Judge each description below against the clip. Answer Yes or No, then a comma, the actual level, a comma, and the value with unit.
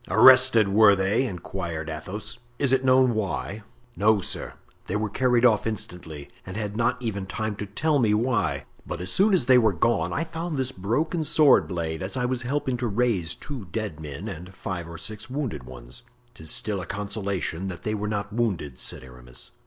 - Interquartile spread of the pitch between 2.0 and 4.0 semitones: No, average, 5.2 semitones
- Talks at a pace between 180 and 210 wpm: Yes, average, 195 wpm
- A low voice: Yes, low, 105 Hz